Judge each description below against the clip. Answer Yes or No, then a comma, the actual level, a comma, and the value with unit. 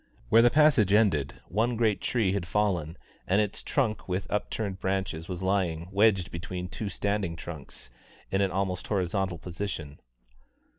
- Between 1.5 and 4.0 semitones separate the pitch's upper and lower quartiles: Yes, average, 3.1 semitones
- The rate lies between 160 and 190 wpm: No, average, 150 wpm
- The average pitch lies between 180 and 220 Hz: No, very low, 95 Hz